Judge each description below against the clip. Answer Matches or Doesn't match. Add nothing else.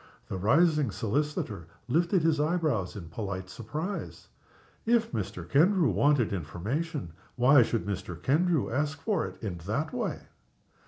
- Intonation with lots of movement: Matches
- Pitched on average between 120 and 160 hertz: Matches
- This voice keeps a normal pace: Doesn't match